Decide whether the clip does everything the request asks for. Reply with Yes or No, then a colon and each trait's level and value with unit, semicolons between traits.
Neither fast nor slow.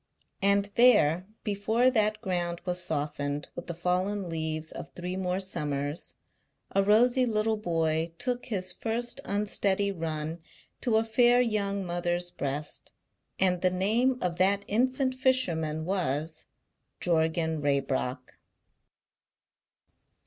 No: slow, 120 wpm